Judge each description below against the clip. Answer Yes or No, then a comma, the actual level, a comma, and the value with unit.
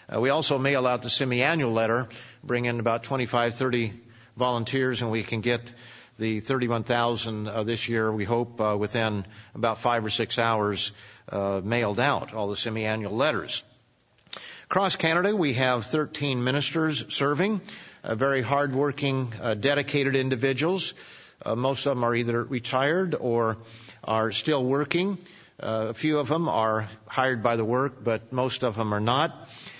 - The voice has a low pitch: Yes, low, 120 Hz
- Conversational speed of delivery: Yes, average, 160 wpm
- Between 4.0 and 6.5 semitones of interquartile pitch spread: No, average, 3.5 semitones